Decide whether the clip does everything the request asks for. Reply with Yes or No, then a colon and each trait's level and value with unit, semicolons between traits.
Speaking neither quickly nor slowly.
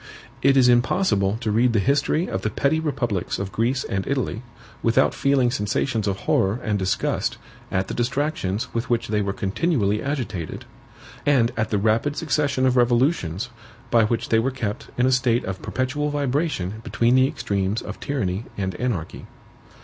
Yes: average, 170 wpm